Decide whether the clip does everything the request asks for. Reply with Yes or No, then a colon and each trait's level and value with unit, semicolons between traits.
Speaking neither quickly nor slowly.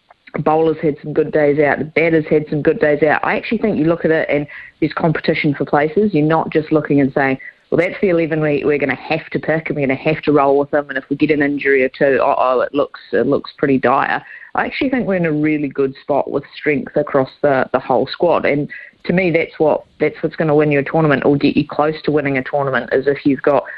No: fast, 275 wpm